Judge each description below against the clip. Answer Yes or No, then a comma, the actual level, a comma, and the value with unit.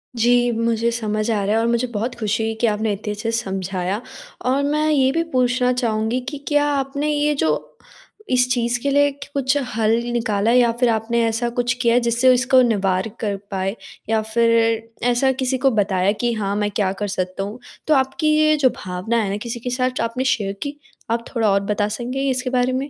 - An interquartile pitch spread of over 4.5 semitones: No, average, 3.3 semitones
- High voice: Yes, high, 235 Hz